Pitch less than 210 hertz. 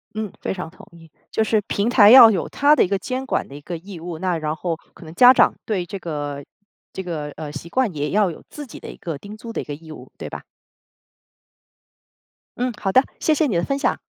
Yes: medium, 185 Hz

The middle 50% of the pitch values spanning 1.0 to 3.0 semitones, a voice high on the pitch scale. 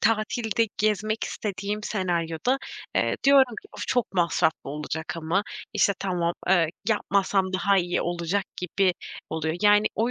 No: average, 3.8 semitones; high, 195 Hz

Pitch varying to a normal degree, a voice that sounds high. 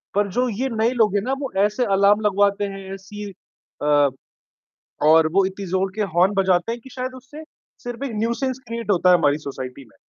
Yes: average, 4.0 semitones; high, 205 Hz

